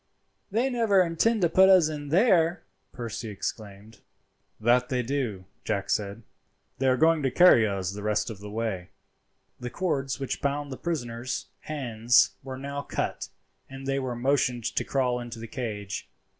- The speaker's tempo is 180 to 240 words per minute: No, average, 165 wpm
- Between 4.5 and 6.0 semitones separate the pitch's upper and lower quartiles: Yes, average, 5.1 semitones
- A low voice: Yes, low, 130 Hz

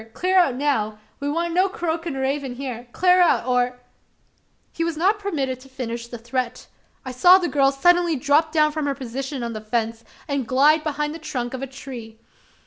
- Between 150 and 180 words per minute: No, average, 200 wpm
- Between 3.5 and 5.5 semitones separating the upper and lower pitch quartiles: Yes, average, 4.5 semitones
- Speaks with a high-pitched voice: Yes, very high, 275 Hz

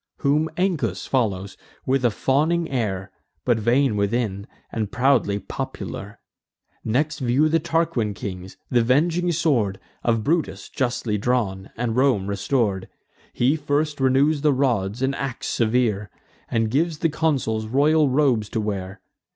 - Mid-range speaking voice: No, low, 125 Hz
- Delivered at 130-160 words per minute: Yes, slow, 135 wpm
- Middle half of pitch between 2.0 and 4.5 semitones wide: No, wide, 5.4 semitones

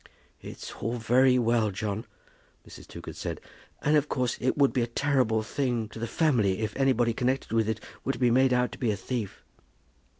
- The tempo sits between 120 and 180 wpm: No, average, 190 wpm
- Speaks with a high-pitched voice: No, low, 120 Hz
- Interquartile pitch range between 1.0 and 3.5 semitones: Yes, average, 2.9 semitones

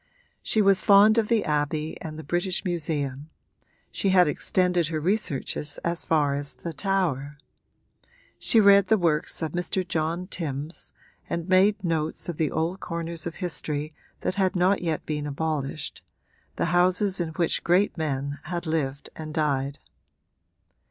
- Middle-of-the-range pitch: Yes, medium, 165 Hz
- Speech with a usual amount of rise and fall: Yes, average, 3.4 semitones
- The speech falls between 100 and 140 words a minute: No, average, 150 wpm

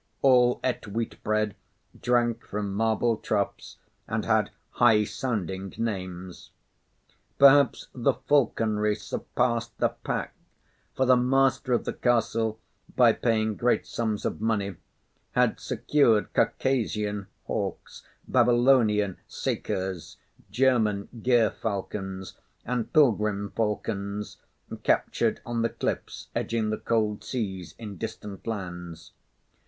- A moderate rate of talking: No, slow, 105 wpm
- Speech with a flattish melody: No, average, 3.0 semitones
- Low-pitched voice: Yes, low, 110 Hz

